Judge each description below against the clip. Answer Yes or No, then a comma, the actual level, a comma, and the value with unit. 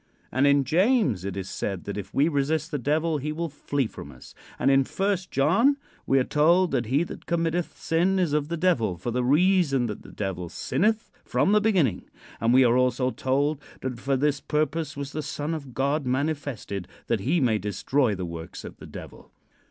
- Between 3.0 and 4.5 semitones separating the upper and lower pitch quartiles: No, average, 5.0 semitones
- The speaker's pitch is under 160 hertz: Yes, medium, 140 Hz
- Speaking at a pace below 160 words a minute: No, fast, 205 wpm